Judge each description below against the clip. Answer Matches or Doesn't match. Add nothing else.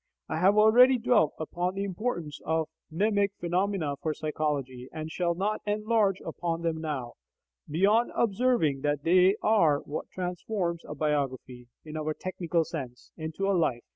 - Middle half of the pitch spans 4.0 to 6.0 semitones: Matches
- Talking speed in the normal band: Matches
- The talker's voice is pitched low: Doesn't match